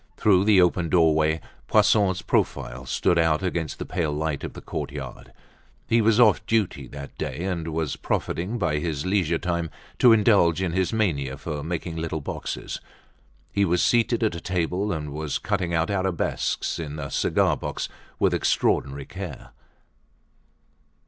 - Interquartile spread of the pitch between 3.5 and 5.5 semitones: Yes, average, 3.8 semitones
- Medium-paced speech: Yes, average, 155 wpm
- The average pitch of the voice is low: Yes, very low, 85 Hz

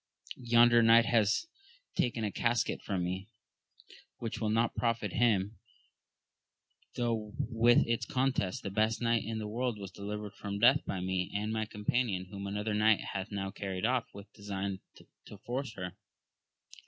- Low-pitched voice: Yes, low, 110 Hz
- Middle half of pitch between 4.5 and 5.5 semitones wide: No, average, 2.8 semitones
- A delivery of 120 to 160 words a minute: Yes, average, 155 wpm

